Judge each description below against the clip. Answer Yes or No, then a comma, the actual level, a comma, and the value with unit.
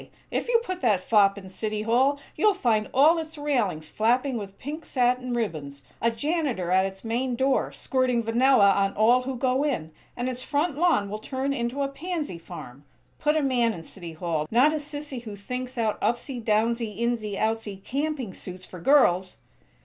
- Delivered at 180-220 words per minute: Yes, average, 185 wpm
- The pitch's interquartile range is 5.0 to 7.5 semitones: Yes, average, 5.3 semitones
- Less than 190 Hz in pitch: No, high, 240 Hz